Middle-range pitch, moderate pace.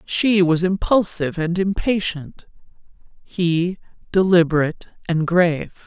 No: medium, 175 Hz; slow, 90 wpm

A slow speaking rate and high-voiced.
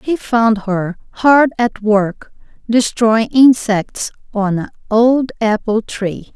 Yes: slow, 125 wpm; high, 225 Hz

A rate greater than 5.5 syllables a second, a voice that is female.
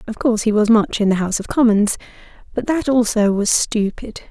Yes: 5.7 syllables/s; female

